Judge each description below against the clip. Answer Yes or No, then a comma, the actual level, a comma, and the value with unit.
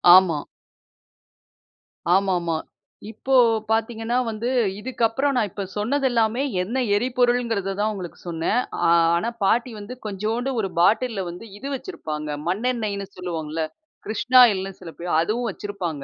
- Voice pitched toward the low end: No, high, 215 Hz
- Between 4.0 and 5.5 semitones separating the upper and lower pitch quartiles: Yes, average, 4.6 semitones